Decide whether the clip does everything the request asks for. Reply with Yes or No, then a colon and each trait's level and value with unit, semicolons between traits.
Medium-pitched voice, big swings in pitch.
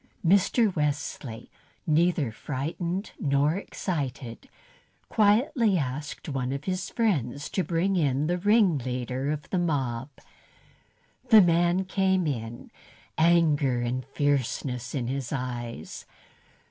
Yes: medium, 150 Hz; wide, 5.8 semitones